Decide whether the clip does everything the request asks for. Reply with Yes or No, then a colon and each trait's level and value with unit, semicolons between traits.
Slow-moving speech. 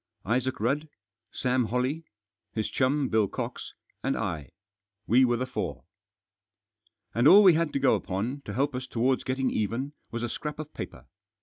No: average, 170 wpm